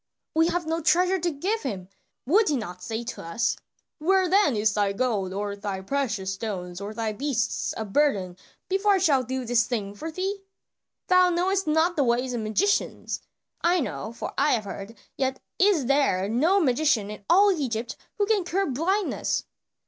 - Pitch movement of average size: No, wide, 8.6 semitones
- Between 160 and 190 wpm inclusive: Yes, average, 180 wpm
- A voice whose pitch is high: Yes, very high, 265 Hz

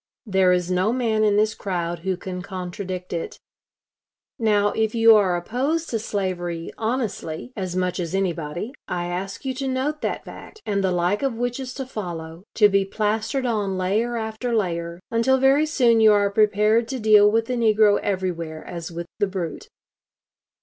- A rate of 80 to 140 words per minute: No, average, 175 wpm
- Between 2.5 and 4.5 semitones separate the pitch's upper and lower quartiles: Yes, average, 4.1 semitones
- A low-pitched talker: No, high, 205 Hz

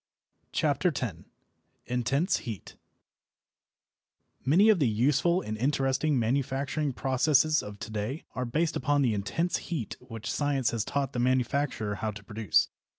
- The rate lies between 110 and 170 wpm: Yes, average, 140 wpm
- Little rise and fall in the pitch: No, average, 4.4 semitones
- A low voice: Yes, low, 130 Hz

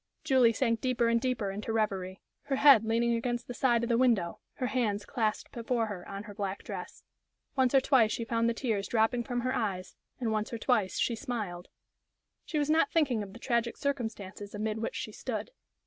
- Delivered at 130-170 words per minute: No, fast, 205 wpm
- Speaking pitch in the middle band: No, high, 230 Hz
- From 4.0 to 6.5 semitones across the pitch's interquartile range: No, average, 2.8 semitones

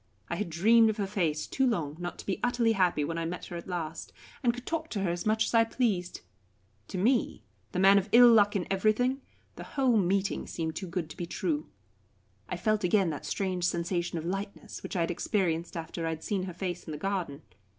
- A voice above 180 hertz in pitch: Yes, high, 190 Hz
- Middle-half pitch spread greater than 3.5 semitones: Yes, average, 4.0 semitones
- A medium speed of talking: No, fast, 230 wpm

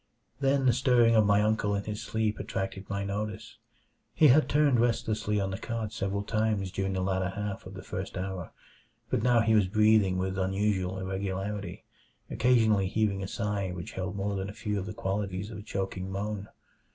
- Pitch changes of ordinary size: No, narrow, 2.2 semitones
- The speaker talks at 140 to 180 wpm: No, average, 190 wpm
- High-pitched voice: No, low, 100 Hz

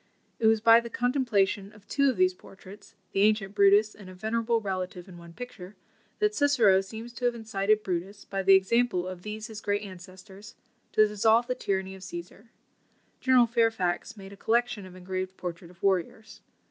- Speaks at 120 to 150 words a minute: No, average, 185 wpm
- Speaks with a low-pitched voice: No, high, 205 Hz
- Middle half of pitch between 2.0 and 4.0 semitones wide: Yes, average, 3.3 semitones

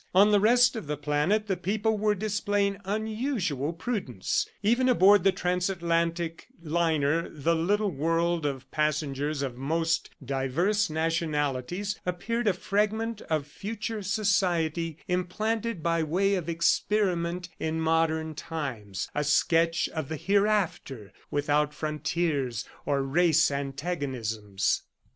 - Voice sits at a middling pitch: Yes, medium, 170 Hz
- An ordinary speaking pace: No, slow, 120 wpm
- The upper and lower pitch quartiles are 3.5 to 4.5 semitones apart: No, average, 5.3 semitones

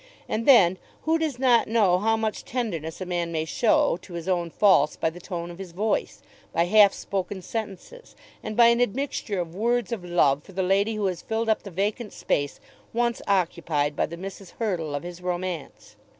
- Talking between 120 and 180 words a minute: No, average, 200 wpm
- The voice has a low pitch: No, high, 195 Hz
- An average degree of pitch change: Yes, average, 4.5 semitones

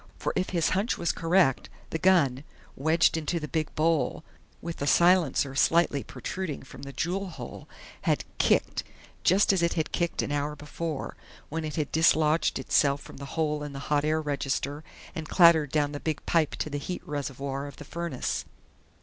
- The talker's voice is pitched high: No, medium, 155 Hz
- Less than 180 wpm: No, average, 185 wpm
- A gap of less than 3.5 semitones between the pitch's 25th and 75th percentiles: Yes, average, 2.9 semitones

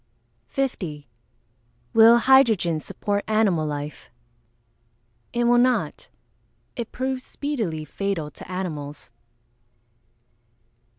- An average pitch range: No, wide, 7.5 semitones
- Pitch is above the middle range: Yes, high, 205 Hz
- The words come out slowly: Yes, slow, 80 wpm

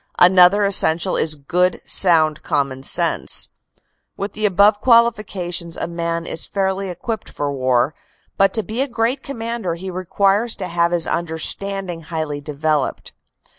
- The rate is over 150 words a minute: No, average, 140 wpm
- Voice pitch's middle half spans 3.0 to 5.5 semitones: Yes, average, 3.9 semitones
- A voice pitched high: No, medium, 180 Hz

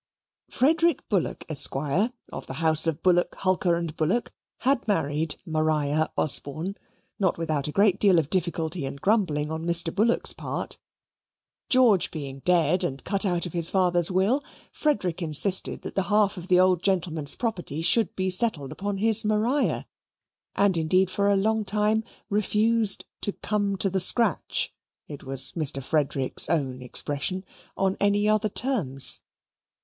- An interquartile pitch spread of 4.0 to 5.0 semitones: Yes, average, 4.7 semitones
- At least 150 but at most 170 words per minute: Yes, average, 155 wpm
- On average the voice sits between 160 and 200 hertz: Yes, medium, 185 Hz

